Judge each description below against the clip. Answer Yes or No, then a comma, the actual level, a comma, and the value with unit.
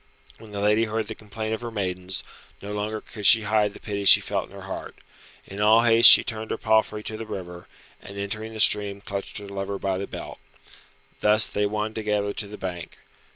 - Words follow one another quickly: Yes, fast, 215 wpm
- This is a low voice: Yes, low, 105 Hz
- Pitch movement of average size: No, narrow, 1.5 semitones